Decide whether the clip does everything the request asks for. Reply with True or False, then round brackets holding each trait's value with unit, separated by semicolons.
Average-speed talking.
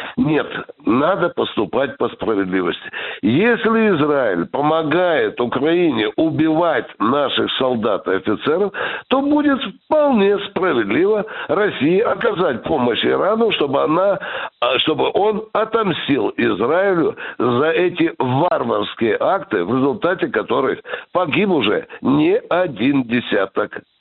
False (100 wpm)